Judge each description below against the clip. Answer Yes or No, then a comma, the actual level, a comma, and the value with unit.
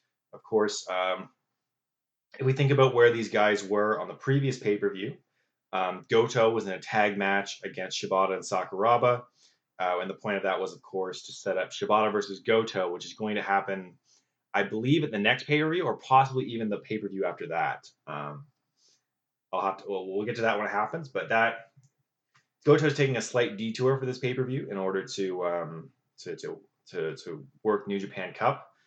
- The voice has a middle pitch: No, low, 110 Hz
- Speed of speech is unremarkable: No, fast, 210 wpm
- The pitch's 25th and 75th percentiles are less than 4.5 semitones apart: No, average, 5.0 semitones